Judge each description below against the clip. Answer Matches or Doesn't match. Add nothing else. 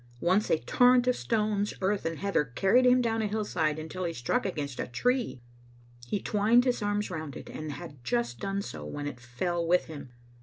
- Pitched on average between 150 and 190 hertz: Matches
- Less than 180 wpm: Doesn't match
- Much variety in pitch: Matches